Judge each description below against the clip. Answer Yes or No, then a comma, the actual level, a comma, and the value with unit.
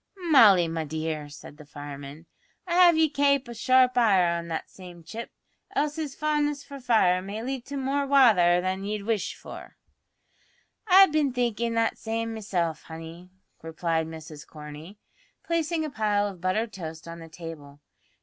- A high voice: Yes, high, 205 Hz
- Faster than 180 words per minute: No, average, 165 wpm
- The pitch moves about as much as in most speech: No, wide, 8.2 semitones